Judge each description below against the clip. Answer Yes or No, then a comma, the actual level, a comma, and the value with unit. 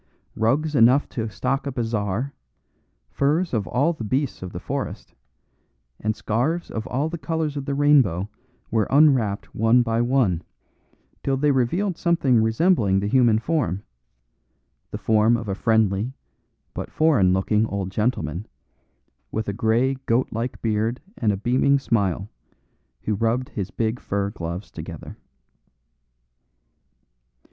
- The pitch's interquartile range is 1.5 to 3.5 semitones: No, average, 4.6 semitones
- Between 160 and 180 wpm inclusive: No, slow, 135 wpm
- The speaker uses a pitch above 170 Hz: No, low, 115 Hz